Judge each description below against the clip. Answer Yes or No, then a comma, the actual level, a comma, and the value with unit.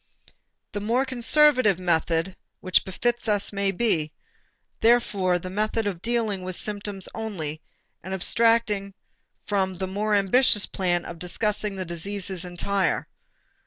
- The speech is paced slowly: Yes, slow, 125 wpm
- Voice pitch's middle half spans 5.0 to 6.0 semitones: No, average, 3.0 semitones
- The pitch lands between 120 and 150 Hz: No, high, 200 Hz